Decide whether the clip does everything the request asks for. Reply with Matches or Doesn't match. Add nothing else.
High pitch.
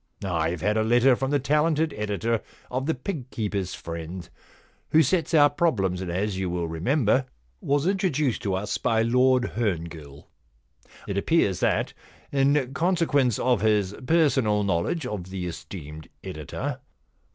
Doesn't match